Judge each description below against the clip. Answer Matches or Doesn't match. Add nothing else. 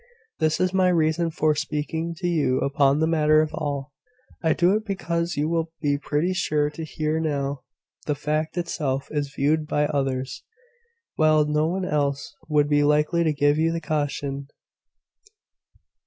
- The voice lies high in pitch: Doesn't match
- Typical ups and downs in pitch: Doesn't match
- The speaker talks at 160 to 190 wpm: Matches